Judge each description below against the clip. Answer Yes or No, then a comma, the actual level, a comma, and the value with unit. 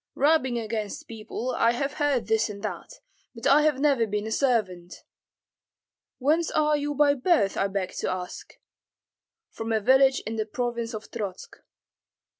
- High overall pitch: Yes, high, 235 Hz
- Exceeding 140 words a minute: Yes, average, 160 wpm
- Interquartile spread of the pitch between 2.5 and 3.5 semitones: No, average, 4.6 semitones